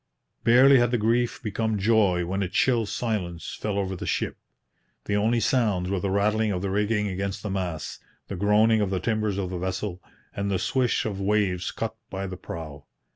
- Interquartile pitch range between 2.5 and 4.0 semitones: Yes, average, 2.9 semitones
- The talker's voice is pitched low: Yes, low, 100 Hz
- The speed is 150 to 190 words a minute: No, average, 200 wpm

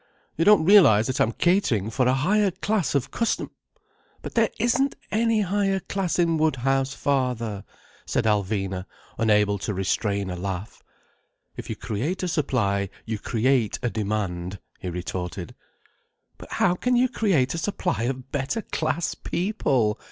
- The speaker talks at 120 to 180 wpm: Yes, average, 150 wpm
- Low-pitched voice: Yes, low, 130 Hz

